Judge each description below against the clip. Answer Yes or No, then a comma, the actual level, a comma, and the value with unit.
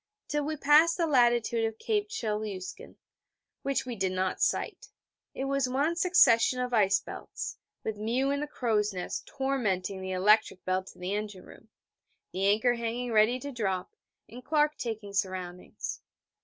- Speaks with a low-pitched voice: No, high, 230 Hz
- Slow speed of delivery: No, average, 160 wpm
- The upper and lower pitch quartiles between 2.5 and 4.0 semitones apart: No, wide, 5.5 semitones